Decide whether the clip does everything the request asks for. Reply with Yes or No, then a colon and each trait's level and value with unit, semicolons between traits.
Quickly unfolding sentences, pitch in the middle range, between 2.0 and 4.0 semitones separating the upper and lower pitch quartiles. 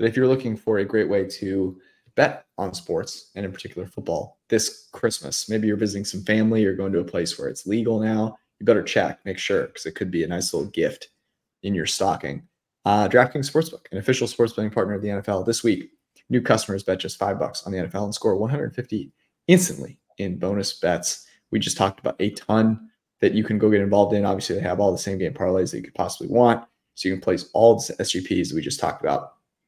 No: fast, 230 wpm; low, 105 Hz; average, 2.9 semitones